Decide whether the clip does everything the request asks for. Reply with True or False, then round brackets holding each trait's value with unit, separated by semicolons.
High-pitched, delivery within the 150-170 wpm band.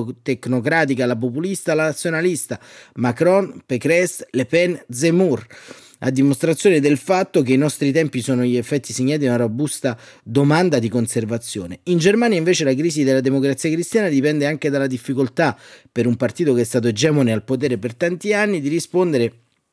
False (140 Hz; 165 wpm)